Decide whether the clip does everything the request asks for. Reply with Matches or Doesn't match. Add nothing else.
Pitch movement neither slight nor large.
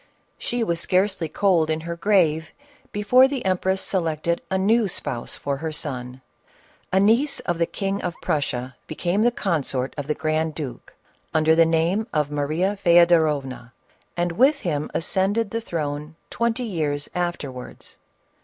Matches